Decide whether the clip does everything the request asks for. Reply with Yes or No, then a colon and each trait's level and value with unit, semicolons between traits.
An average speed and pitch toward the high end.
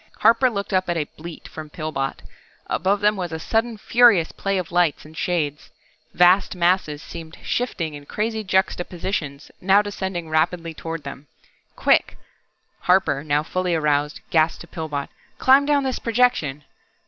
No: average, 150 wpm; medium, 175 Hz